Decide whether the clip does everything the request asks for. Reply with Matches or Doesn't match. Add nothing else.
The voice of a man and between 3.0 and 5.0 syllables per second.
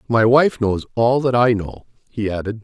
Matches